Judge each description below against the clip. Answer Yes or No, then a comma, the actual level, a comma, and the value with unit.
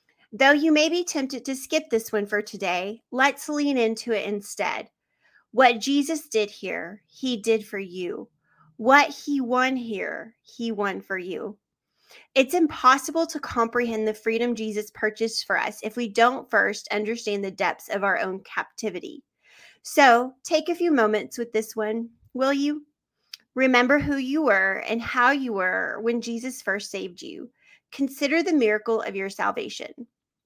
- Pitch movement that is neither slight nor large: Yes, average, 4.6 semitones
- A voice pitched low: No, high, 235 Hz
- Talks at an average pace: Yes, average, 160 wpm